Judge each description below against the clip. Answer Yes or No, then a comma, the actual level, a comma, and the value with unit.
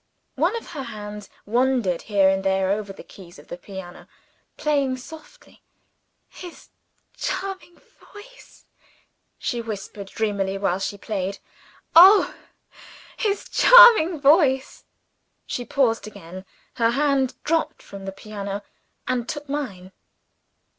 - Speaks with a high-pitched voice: Yes, high, 235 Hz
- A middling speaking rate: No, slow, 120 wpm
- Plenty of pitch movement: Yes, wide, 7.4 semitones